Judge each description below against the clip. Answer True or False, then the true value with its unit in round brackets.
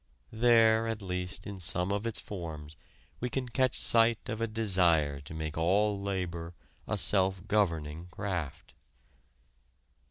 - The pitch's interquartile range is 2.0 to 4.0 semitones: False (4.6 semitones)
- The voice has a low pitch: True (95 Hz)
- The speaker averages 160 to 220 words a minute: False (135 wpm)